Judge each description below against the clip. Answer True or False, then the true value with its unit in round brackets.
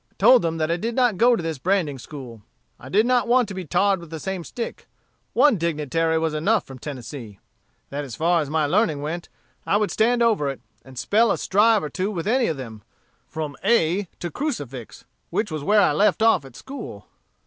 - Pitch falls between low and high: True (170 Hz)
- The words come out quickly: True (225 wpm)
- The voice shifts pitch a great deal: True (6.8 semitones)